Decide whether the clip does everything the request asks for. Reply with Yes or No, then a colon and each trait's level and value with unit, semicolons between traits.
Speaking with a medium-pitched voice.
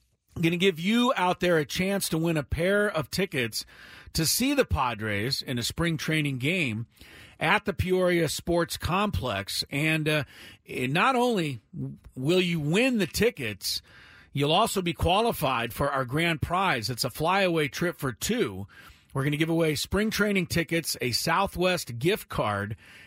Yes: medium, 160 Hz